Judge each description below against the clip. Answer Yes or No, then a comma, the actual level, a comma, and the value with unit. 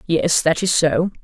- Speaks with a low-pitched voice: No, medium, 165 Hz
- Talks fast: No, average, 195 wpm